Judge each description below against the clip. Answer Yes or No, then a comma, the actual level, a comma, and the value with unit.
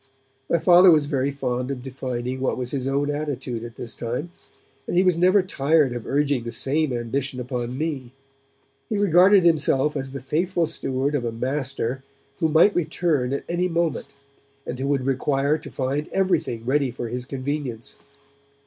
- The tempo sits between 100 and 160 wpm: No, average, 175 wpm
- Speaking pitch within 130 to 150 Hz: Yes, medium, 140 Hz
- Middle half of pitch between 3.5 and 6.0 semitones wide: Yes, average, 3.8 semitones